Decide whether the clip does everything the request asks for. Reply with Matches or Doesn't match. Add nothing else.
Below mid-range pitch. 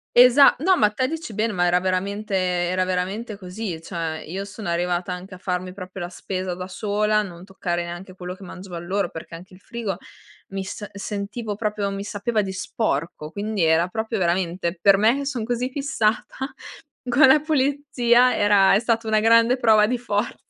Doesn't match